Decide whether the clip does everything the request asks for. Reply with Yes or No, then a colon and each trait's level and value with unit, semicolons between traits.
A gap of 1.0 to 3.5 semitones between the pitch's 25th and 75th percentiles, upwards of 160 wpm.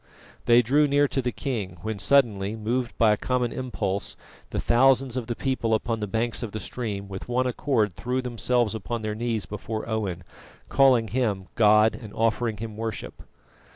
Yes: average, 2.8 semitones; average, 180 wpm